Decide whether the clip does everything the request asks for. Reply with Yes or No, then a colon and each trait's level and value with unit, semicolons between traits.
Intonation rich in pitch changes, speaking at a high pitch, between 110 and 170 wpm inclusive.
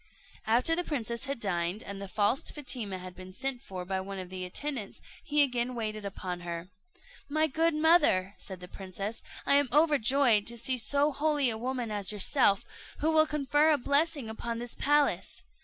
No: wide, 6.5 semitones; high, 235 Hz; average, 185 wpm